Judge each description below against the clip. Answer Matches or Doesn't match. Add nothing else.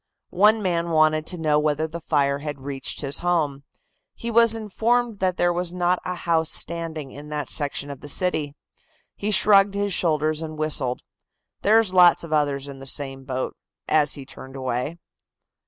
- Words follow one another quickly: Doesn't match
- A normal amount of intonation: Matches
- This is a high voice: Doesn't match